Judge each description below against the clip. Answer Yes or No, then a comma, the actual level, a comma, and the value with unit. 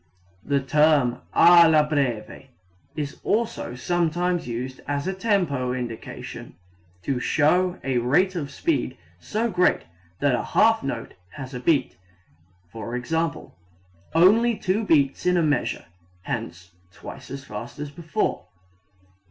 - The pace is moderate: No, slow, 125 wpm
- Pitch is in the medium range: Yes, medium, 150 Hz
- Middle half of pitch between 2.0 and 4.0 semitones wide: No, wide, 5.6 semitones